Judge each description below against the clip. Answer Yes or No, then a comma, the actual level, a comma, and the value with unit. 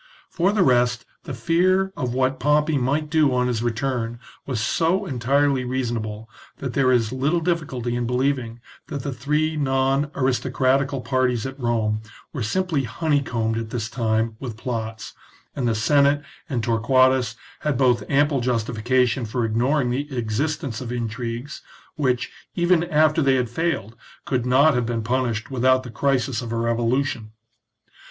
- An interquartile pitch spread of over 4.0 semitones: No, average, 3.3 semitones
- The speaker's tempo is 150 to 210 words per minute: Yes, average, 155 wpm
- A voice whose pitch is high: No, low, 130 Hz